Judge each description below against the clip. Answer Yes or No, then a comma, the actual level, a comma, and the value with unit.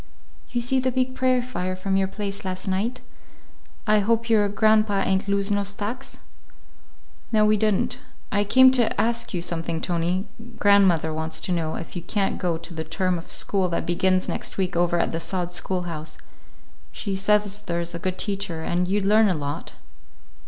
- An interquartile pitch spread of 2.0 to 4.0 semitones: Yes, average, 3.4 semitones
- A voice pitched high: Yes, high, 195 Hz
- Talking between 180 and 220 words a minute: Yes, average, 185 wpm